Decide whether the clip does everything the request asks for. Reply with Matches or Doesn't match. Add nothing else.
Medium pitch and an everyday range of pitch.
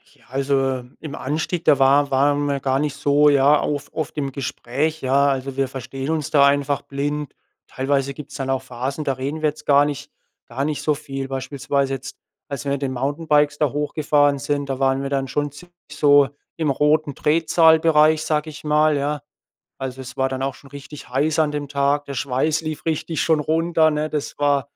Doesn't match